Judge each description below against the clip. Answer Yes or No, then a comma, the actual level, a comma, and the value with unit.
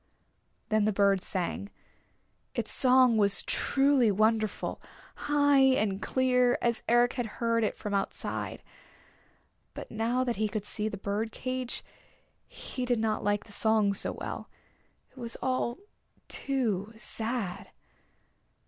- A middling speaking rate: No, slow, 130 wpm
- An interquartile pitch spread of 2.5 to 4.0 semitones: Yes, average, 3.4 semitones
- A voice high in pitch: Yes, high, 225 Hz